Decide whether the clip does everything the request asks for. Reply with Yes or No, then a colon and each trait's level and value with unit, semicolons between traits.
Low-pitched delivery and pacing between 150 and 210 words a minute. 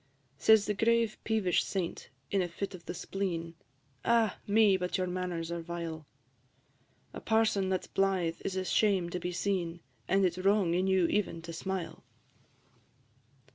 No: medium, 185 Hz; average, 170 wpm